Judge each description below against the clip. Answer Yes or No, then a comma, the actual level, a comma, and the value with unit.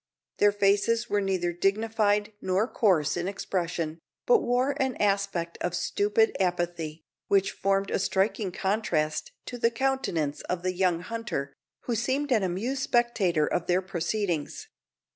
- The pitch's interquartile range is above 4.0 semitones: Yes, average, 4.4 semitones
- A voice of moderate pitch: No, high, 195 Hz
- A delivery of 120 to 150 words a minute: Yes, average, 140 wpm